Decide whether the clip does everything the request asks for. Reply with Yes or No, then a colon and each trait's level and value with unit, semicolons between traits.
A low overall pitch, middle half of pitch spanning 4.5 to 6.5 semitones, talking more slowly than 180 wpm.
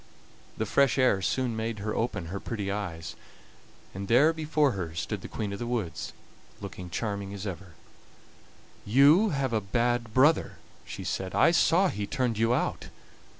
Yes: low, 110 Hz; average, 4.9 semitones; average, 170 wpm